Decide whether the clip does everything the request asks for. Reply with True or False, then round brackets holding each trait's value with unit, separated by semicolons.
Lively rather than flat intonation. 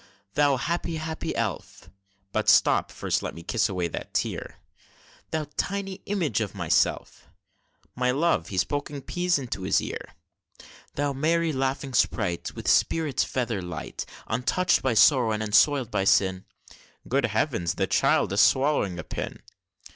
True (6.8 semitones)